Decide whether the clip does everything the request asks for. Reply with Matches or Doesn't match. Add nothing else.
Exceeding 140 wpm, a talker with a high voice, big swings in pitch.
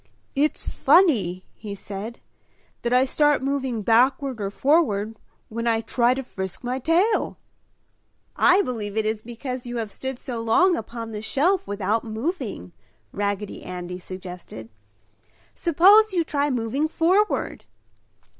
Doesn't match